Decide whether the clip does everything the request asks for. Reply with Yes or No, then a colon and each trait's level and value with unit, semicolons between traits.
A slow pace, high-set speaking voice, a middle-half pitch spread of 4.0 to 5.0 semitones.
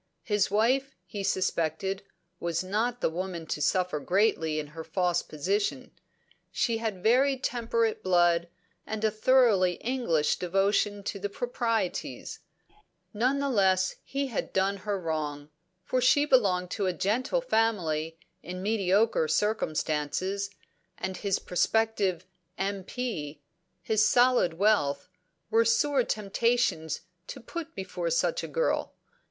Yes: slow, 125 wpm; high, 200 Hz; average, 4.5 semitones